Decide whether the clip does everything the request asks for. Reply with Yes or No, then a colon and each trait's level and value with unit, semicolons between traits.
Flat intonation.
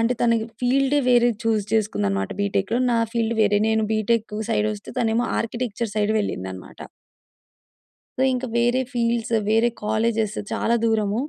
Yes: narrow, 1.9 semitones